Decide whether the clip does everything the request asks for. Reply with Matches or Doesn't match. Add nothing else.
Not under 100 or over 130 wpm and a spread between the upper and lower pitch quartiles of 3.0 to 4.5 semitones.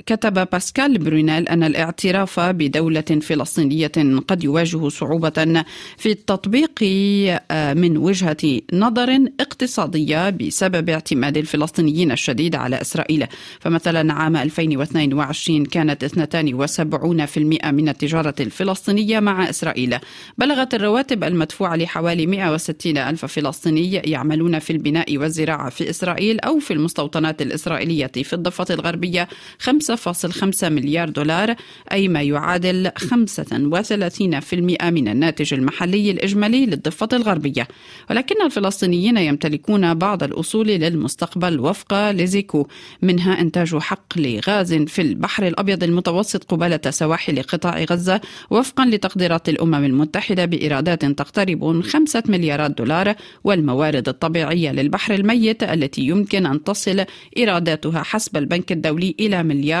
Matches